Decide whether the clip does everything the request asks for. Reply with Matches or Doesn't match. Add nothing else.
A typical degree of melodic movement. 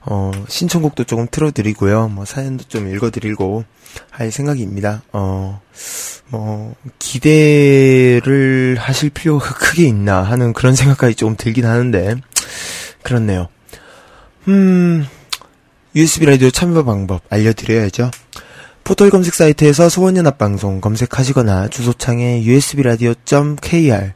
Matches